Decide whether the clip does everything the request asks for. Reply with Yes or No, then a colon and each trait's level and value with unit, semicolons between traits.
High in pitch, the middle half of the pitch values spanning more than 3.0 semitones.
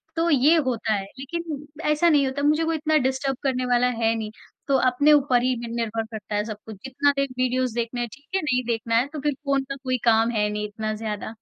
Yes: very high, 255 Hz; average, 4.1 semitones